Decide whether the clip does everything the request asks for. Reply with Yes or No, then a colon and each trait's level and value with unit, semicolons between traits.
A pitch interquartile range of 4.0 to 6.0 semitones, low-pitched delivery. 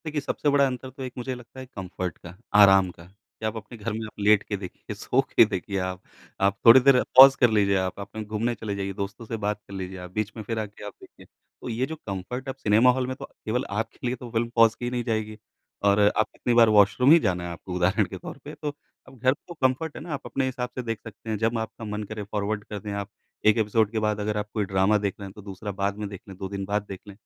No: average, 3.5 semitones; low, 110 Hz